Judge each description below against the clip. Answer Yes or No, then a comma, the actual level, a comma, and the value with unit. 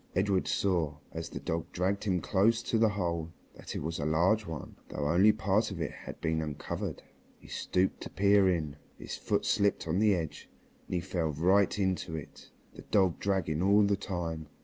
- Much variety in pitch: No, average, 3.7 semitones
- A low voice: Yes, very low, 90 Hz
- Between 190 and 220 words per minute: Yes, average, 195 wpm